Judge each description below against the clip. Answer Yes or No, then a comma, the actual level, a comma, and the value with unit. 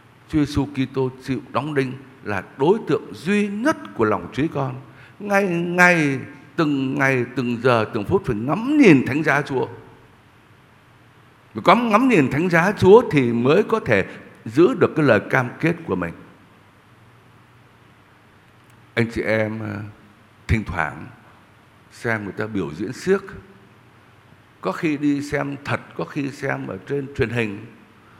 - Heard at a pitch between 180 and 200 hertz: No, low, 130 Hz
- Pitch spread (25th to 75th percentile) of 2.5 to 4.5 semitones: No, average, 4.9 semitones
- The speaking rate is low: Yes, slow, 150 wpm